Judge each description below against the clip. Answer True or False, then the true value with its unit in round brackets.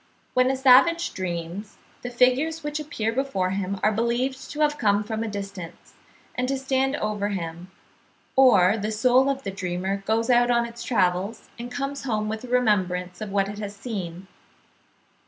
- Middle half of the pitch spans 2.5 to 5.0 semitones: True (4.7 semitones)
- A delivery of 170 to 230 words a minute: True (175 wpm)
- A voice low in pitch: False (220 Hz)